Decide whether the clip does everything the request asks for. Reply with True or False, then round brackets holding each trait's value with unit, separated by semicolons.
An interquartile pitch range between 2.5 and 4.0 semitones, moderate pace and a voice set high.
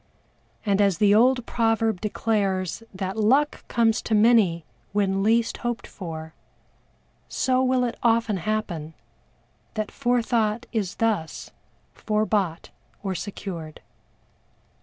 False (3.3 semitones; 115 wpm; 215 Hz)